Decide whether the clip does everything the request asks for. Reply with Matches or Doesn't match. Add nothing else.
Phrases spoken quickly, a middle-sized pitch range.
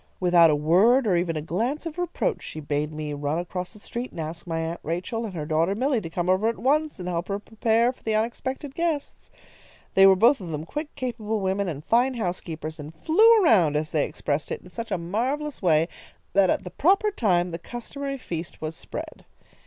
Doesn't match